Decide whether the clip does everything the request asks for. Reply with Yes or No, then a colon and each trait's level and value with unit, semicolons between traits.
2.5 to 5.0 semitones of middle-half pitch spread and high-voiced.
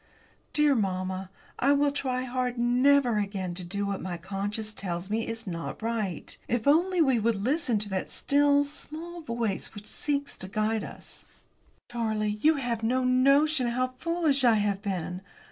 No: wide, 5.6 semitones; high, 235 Hz